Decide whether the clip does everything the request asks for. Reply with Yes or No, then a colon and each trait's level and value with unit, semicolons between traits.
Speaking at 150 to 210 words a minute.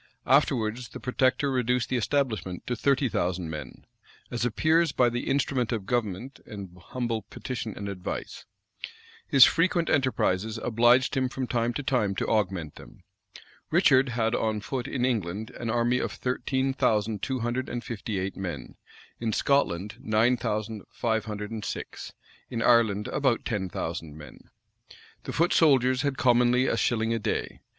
Yes: average, 160 wpm